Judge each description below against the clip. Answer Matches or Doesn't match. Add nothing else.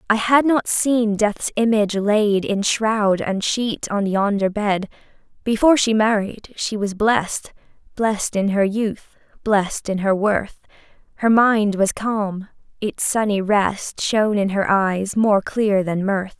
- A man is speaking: Doesn't match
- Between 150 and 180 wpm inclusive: Matches